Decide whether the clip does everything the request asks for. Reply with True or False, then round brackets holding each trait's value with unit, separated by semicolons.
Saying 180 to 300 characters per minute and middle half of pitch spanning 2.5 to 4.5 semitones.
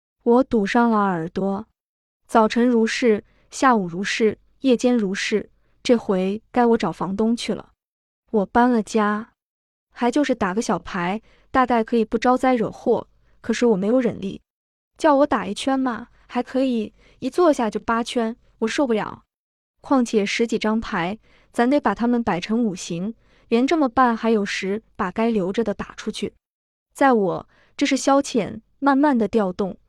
True (230 characters per minute; 2.9 semitones)